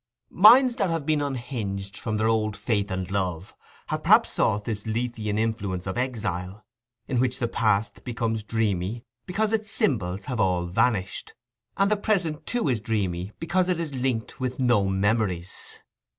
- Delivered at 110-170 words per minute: Yes, average, 165 wpm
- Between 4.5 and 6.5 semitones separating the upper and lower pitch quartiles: Yes, average, 5.0 semitones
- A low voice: Yes, low, 115 Hz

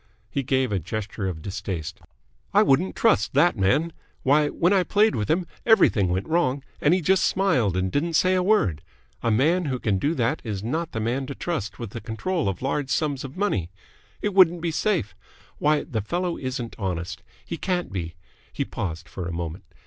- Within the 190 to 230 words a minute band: Yes, average, 200 wpm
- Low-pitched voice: Yes, low, 130 Hz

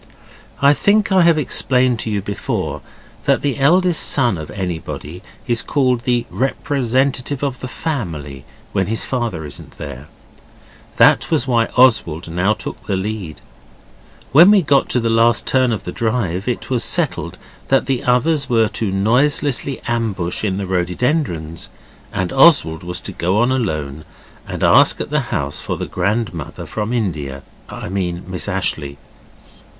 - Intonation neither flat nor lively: No, wide, 6.7 semitones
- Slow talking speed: No, average, 155 wpm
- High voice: No, low, 115 Hz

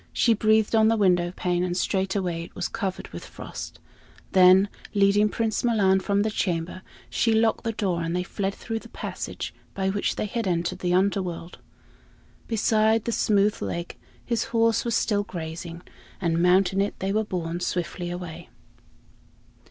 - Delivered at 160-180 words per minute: Yes, average, 165 wpm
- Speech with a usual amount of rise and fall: Yes, average, 3.4 semitones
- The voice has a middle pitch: No, high, 195 Hz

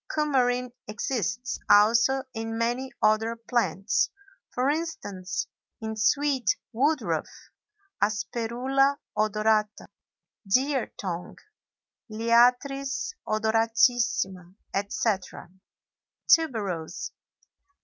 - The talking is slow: Yes, slow, 65 wpm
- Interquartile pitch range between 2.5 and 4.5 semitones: Yes, average, 3.5 semitones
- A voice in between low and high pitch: No, high, 230 Hz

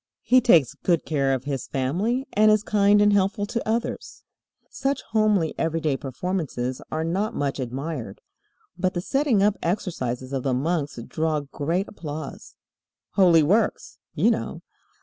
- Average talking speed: Yes, average, 150 wpm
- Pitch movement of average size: No, wide, 6.7 semitones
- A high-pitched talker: No, medium, 165 Hz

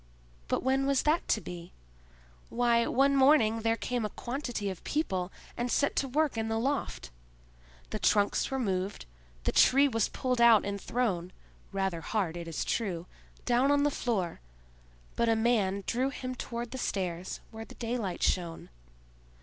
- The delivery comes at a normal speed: Yes, average, 160 wpm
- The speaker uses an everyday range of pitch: Yes, average, 4.8 semitones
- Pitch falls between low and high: No, high, 230 Hz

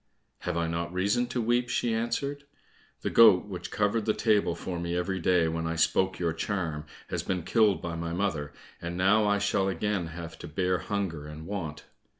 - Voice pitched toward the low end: Yes, very low, 90 Hz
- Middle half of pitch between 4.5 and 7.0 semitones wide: No, average, 3.8 semitones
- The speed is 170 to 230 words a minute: Yes, average, 195 wpm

